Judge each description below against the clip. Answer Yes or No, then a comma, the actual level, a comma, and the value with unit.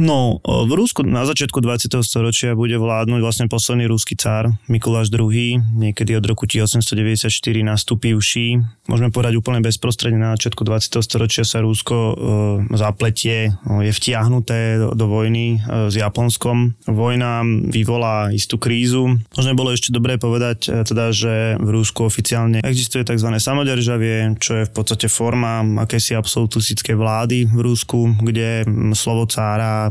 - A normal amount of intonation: No, narrow, 1.3 semitones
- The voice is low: Yes, low, 115 Hz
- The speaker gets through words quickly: No, average, 140 wpm